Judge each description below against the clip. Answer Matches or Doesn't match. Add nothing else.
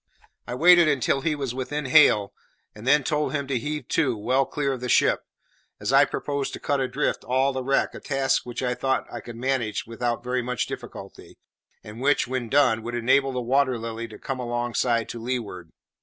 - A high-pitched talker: Doesn't match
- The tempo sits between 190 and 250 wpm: Matches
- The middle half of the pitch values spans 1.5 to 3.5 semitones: Matches